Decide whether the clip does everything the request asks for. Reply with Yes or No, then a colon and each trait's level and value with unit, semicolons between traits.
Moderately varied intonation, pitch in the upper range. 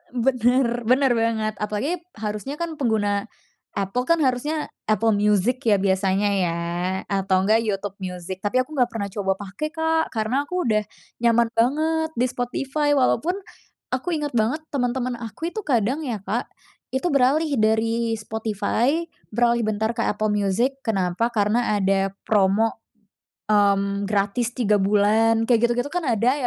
Yes: average, 3.8 semitones; high, 225 Hz